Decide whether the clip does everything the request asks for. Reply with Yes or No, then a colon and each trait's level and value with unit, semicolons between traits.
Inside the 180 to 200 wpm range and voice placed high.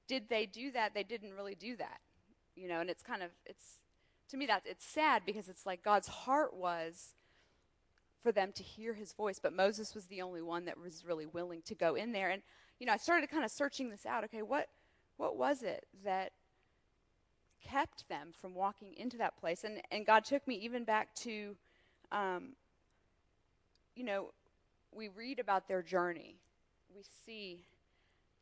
Yes: average, 185 wpm; high, 205 Hz